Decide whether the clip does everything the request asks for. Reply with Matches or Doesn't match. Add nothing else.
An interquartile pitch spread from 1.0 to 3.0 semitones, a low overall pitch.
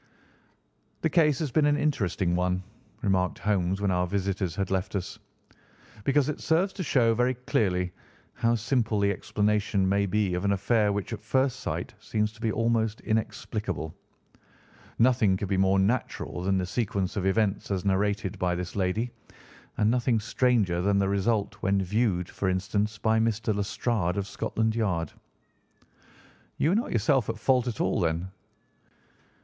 Doesn't match